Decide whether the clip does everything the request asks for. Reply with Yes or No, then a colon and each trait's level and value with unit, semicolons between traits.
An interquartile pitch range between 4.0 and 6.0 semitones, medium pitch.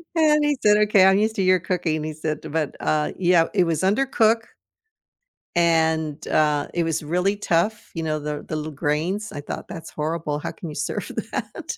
Yes: average, 4.4 semitones; medium, 165 Hz